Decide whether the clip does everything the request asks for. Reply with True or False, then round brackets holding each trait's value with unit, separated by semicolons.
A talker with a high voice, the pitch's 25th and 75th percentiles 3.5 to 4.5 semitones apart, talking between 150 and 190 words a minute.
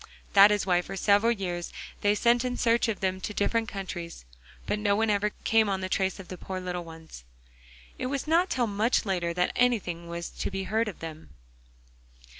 False (200 Hz; 3.9 semitones; 205 wpm)